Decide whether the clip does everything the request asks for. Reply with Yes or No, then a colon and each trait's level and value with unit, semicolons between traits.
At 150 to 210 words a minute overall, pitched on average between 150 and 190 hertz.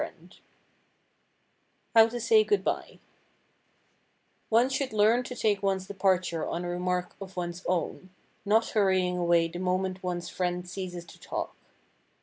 No: average, 140 wpm; medium, 185 Hz